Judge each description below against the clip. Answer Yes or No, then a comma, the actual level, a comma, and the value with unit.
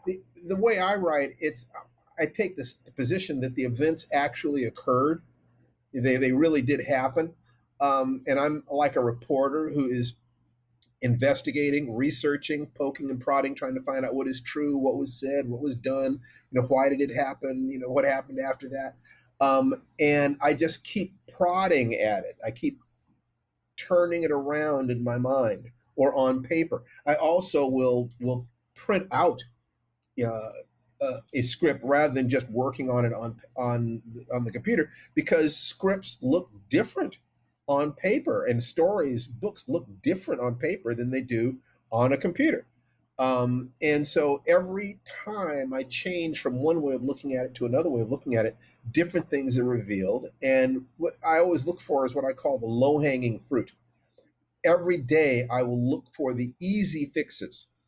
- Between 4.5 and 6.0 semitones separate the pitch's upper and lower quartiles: No, average, 3.5 semitones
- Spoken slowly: No, average, 170 wpm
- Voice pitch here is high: No, low, 135 Hz